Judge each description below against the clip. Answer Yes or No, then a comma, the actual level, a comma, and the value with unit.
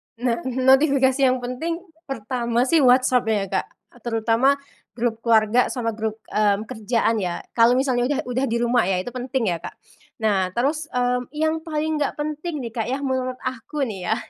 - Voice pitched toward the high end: Yes, very high, 250 Hz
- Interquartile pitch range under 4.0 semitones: Yes, average, 3.0 semitones